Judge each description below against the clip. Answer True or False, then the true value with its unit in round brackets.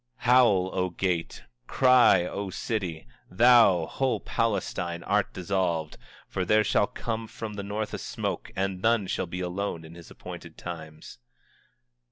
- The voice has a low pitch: True (95 Hz)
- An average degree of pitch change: True (4.0 semitones)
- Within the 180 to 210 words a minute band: False (150 wpm)